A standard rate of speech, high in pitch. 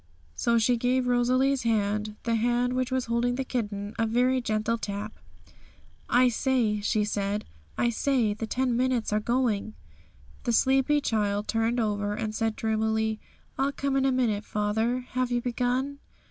Yes: average, 160 wpm; high, 235 Hz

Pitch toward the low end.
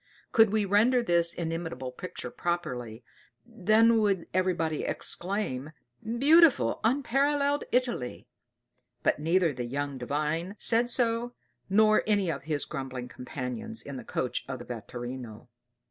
No: medium, 175 Hz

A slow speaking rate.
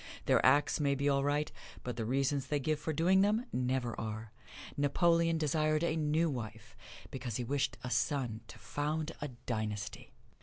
No: average, 175 wpm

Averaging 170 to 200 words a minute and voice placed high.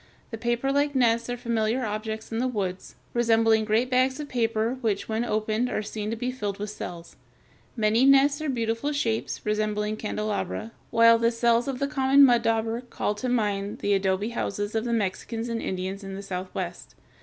Yes: average, 195 wpm; high, 225 Hz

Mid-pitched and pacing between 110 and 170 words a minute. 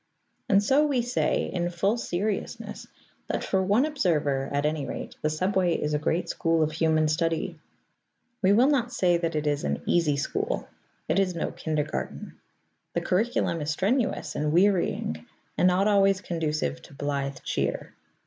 Yes: medium, 170 Hz; average, 165 wpm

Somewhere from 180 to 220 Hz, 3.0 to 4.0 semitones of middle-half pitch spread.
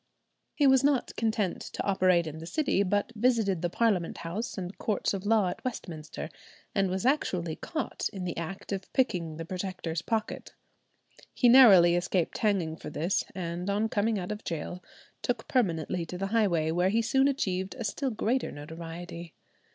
No: high, 190 Hz; average, 4.6 semitones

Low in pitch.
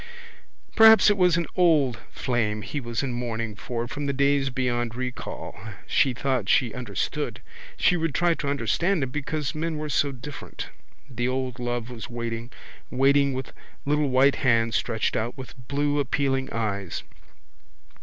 Yes: low, 130 Hz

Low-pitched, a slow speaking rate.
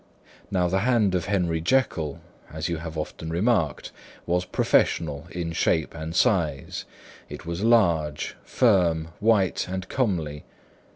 Yes: very low, 85 Hz; slow, 130 wpm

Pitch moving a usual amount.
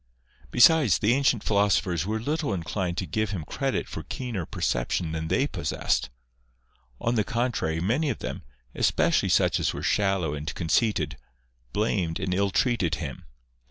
No: wide, 6.2 semitones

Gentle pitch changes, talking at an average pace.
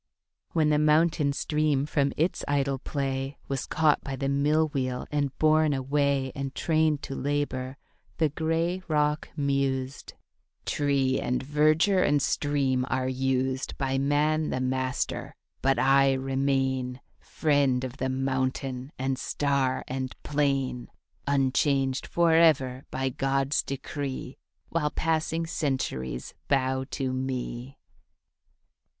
No: narrow, 2.1 semitones; slow, 120 wpm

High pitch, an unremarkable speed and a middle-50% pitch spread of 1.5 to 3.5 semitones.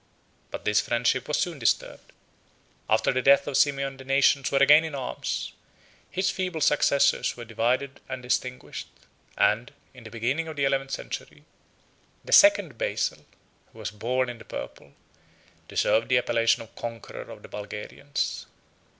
No: low, 130 Hz; average, 155 wpm; average, 3.1 semitones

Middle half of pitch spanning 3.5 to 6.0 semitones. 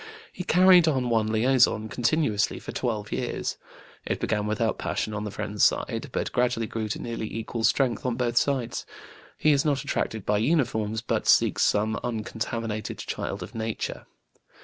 No: narrow, 2.6 semitones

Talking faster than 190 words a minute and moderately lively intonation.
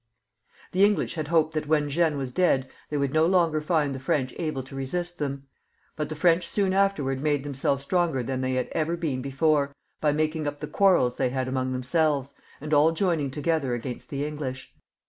Yes: average, 200 wpm; average, 3.4 semitones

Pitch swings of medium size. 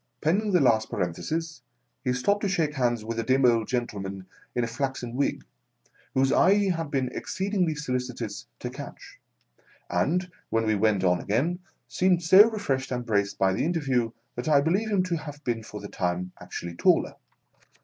No: wide, 6.8 semitones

